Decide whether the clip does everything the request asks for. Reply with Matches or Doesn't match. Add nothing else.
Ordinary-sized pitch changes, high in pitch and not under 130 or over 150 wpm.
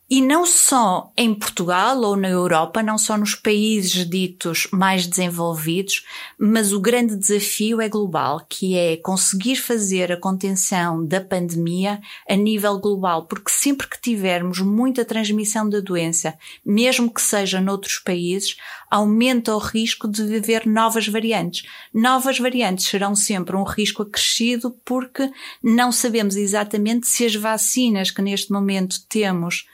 Matches